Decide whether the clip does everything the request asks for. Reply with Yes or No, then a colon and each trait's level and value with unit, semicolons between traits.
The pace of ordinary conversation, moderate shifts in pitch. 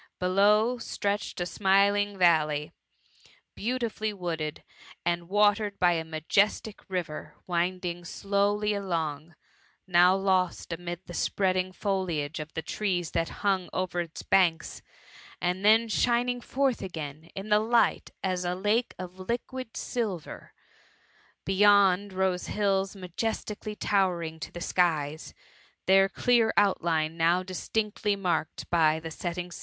No: slow, 130 wpm; average, 3.1 semitones